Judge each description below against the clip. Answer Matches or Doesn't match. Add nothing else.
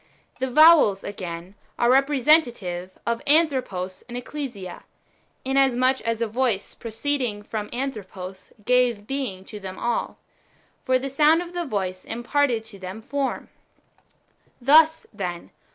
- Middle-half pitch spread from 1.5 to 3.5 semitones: Doesn't match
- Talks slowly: Matches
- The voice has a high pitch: Matches